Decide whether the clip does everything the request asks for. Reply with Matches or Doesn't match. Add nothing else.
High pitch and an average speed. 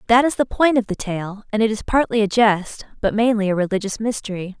Doesn't match